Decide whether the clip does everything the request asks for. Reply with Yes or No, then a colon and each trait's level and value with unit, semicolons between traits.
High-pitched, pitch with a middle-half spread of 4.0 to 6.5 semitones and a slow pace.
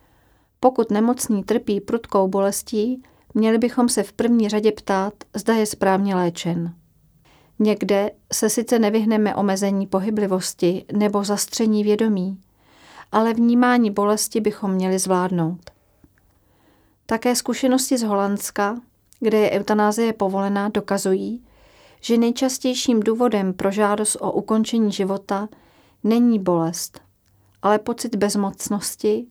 No: high, 210 Hz; average, 2.8 semitones; slow, 110 wpm